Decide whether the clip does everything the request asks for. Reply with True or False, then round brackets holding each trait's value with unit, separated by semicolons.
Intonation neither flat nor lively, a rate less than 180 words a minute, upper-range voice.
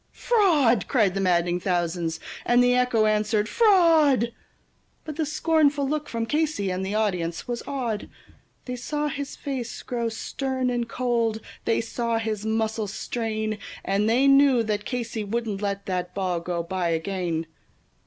True (4.7 semitones; 155 wpm; 225 Hz)